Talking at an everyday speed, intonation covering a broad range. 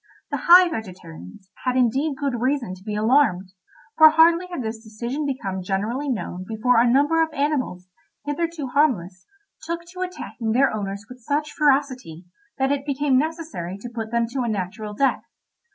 Yes: average, 170 wpm; wide, 5.7 semitones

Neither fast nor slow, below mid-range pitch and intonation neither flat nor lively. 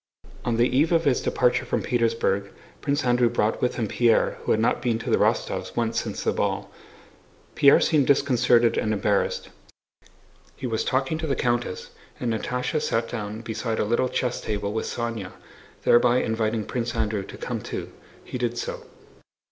No: average, 175 wpm; low, 120 Hz; narrow, 2.1 semitones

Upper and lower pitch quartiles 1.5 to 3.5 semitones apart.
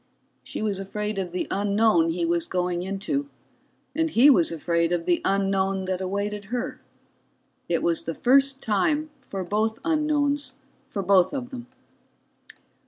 No: wide, 5.6 semitones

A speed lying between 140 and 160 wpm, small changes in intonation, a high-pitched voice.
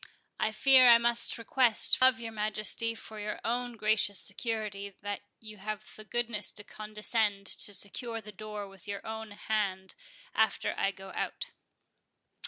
Yes: average, 155 wpm; narrow, 2.0 semitones; high, 215 Hz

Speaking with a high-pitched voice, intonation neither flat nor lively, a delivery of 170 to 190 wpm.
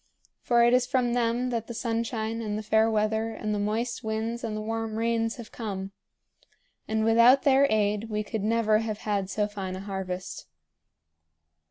No: high, 220 Hz; narrow, 1.7 semitones; average, 180 wpm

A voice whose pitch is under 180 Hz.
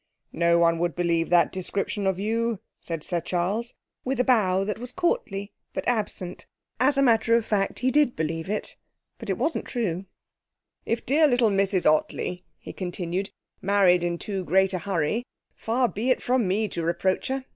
No: high, 195 Hz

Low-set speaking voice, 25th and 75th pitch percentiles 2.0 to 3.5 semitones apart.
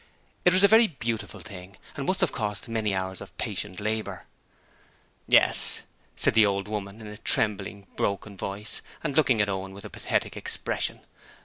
Yes: low, 105 Hz; narrow, 2.4 semitones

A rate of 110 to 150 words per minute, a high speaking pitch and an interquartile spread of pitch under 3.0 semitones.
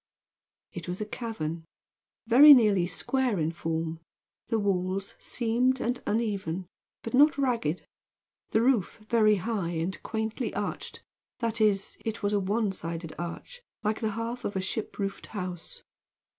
No: average, 145 wpm; high, 210 Hz; average, 4.4 semitones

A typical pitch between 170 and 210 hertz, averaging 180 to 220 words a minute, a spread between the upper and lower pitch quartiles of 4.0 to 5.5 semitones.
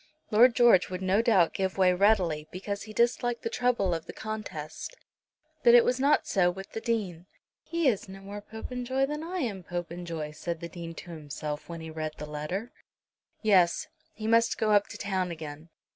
Yes: high, 190 Hz; average, 190 wpm; average, 5.2 semitones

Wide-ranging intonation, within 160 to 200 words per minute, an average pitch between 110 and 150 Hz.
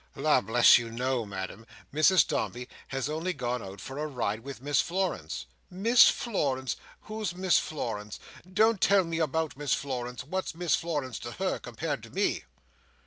Yes: wide, 6.3 semitones; average, 165 wpm; medium, 140 Hz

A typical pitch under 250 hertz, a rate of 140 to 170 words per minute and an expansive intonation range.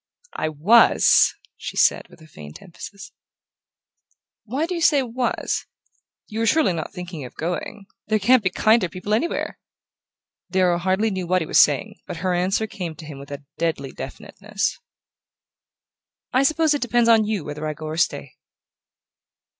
Yes: medium, 185 Hz; average, 160 wpm; wide, 6.1 semitones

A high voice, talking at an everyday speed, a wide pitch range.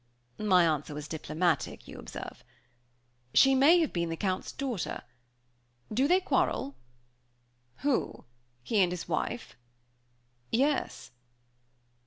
No: high, 200 Hz; slow, 110 wpm; wide, 8.4 semitones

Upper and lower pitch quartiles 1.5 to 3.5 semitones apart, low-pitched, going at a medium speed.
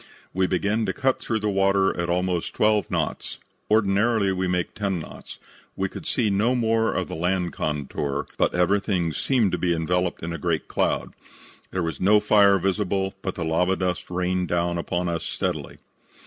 Yes: average, 2.7 semitones; very low, 95 Hz; average, 180 wpm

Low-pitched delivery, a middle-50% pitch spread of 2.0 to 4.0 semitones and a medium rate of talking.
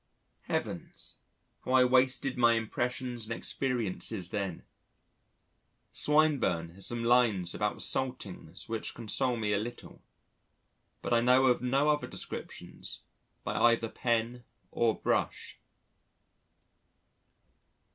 No: low, 120 Hz; narrow, 2.5 semitones; slow, 105 wpm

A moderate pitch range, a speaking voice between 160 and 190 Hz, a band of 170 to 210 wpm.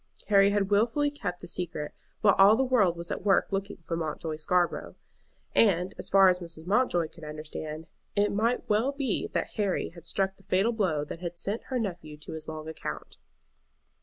Yes: average, 3.9 semitones; medium, 185 Hz; average, 195 wpm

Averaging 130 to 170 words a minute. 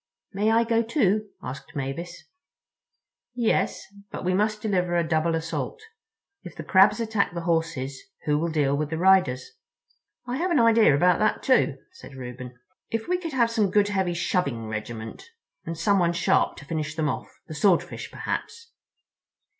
Yes: average, 160 wpm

